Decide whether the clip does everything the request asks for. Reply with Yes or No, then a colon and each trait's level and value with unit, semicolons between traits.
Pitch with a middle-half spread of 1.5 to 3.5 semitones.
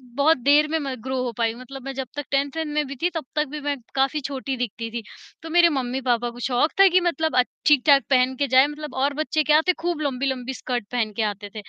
Yes: average, 3.2 semitones